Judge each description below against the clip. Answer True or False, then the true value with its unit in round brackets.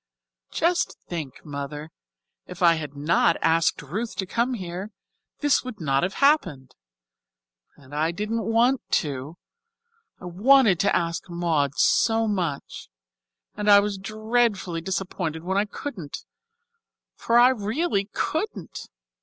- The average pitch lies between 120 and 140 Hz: False (190 Hz)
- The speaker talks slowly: True (130 wpm)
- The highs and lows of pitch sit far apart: True (5.7 semitones)